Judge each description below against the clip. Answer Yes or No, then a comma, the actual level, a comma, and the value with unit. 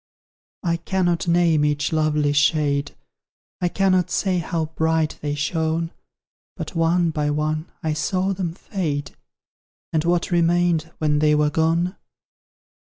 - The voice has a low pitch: No, medium, 160 Hz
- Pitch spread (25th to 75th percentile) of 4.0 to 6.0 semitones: No, narrow, 2.4 semitones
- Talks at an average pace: No, slow, 130 wpm